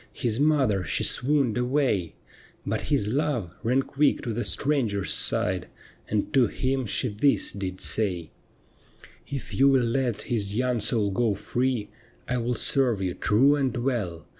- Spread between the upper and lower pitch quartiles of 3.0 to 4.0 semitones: No, average, 4.5 semitones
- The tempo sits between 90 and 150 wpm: No, average, 165 wpm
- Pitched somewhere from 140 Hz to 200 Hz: No, low, 120 Hz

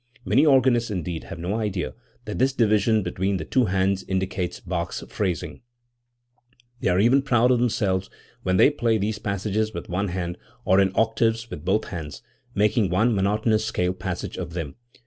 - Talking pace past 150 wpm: Yes, average, 170 wpm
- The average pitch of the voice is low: Yes, low, 100 Hz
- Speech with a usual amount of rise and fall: Yes, average, 3.4 semitones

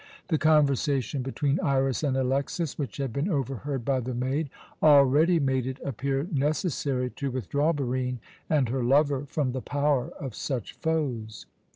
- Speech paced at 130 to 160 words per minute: Yes, average, 155 wpm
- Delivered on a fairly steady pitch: Yes, narrow, 2.2 semitones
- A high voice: No, low, 135 Hz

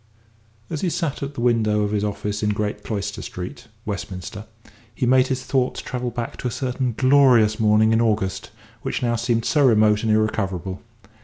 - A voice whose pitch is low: Yes, low, 110 Hz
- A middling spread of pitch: Yes, average, 3.2 semitones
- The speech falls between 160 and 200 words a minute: Yes, average, 180 wpm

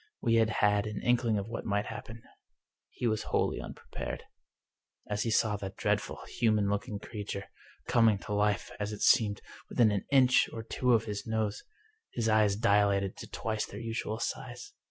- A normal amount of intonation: No, narrow, 1.9 semitones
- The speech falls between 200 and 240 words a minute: No, average, 175 wpm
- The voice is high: No, low, 110 Hz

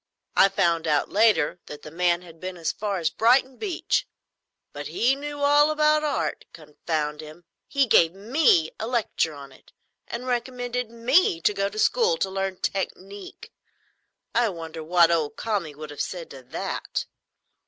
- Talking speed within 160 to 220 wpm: Yes, average, 165 wpm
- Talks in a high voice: Yes, high, 195 Hz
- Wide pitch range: Yes, wide, 7.2 semitones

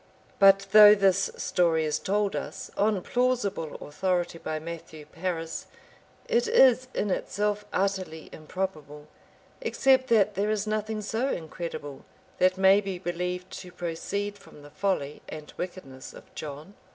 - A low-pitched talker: No, high, 190 Hz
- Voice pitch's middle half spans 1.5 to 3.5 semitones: No, average, 4.2 semitones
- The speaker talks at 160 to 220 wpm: No, average, 140 wpm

